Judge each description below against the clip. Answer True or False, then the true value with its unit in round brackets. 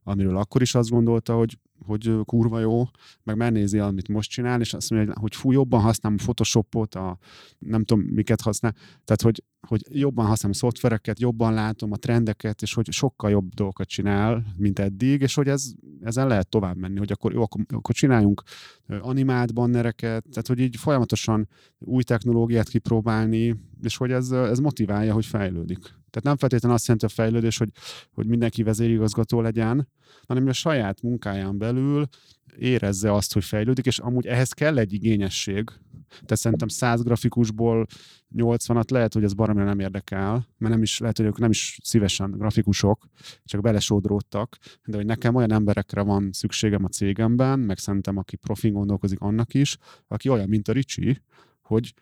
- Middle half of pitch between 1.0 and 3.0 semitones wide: True (2.6 semitones)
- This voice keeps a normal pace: False (170 wpm)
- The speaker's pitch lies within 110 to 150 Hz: True (115 Hz)